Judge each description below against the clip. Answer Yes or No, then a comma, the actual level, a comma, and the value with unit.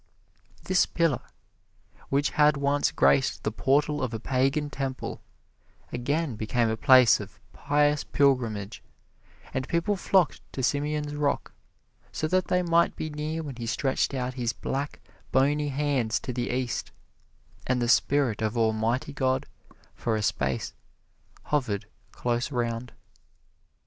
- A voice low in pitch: Yes, low, 130 Hz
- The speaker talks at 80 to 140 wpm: Yes, slow, 135 wpm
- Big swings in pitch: No, average, 3.7 semitones